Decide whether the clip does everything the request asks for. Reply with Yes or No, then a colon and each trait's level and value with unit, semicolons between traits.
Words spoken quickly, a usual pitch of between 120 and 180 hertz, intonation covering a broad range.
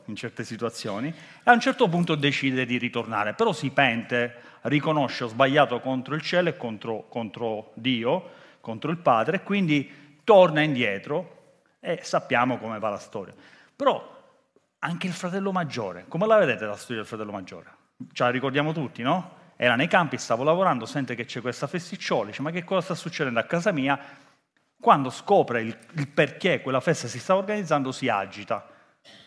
Yes: fast, 175 wpm; low, 135 Hz; wide, 5.7 semitones